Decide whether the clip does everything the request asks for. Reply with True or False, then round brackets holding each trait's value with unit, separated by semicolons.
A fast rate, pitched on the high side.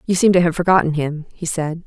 False (260 wpm; 170 Hz)